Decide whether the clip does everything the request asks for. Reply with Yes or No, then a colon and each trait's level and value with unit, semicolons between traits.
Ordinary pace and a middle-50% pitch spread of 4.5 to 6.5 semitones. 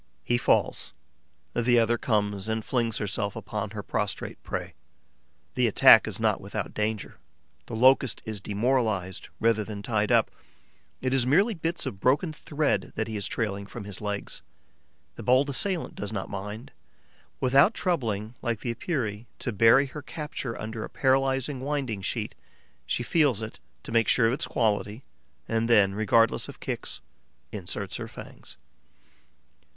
No: average, 155 wpm; average, 4.1 semitones